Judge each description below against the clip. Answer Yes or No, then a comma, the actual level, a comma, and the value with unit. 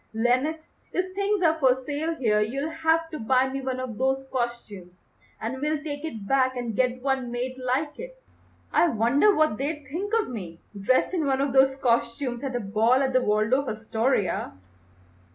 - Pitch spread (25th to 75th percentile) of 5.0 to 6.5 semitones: No, average, 4.0 semitones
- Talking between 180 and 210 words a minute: Yes, average, 185 wpm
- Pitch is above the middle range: Yes, very high, 260 Hz